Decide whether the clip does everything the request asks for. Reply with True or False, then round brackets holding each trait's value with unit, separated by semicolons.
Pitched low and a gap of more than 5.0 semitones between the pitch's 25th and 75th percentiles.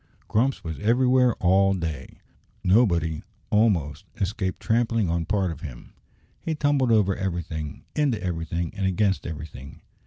True (95 Hz; 5.4 semitones)